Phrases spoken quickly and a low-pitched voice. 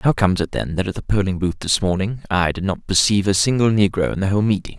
Yes: fast, 275 wpm; low, 100 Hz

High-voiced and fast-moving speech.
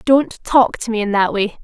Yes: high, 225 Hz; fast, 255 wpm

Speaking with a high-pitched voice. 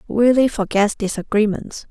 Yes: high, 215 Hz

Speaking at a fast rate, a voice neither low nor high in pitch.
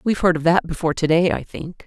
Yes: fast, 290 wpm; medium, 170 Hz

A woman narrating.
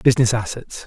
No: male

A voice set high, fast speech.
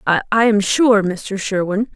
No: high, 205 Hz; average, 155 wpm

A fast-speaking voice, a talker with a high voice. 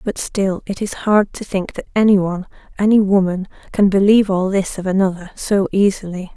No: average, 170 wpm; high, 195 Hz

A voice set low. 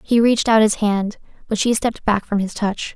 No: high, 215 Hz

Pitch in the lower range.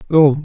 No: medium, 150 Hz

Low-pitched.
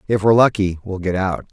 Yes: low, 100 Hz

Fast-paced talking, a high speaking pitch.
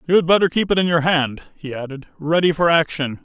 No: fast, 220 wpm; medium, 160 Hz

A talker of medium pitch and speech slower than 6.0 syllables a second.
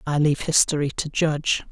Yes: medium, 150 Hz; 5.7 syllables/s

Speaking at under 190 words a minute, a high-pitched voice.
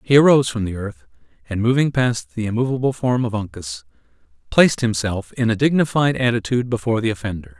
No: average, 175 wpm; low, 115 Hz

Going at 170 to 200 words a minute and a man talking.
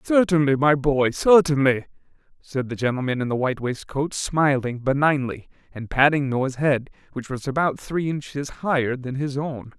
No: average, 160 wpm; male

